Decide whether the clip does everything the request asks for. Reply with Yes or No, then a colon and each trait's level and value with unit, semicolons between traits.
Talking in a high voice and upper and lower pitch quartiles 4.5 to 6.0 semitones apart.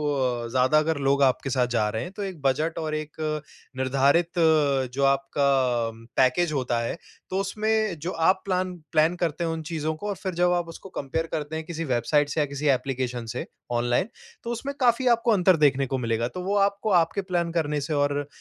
No: medium, 155 Hz; average, 4.8 semitones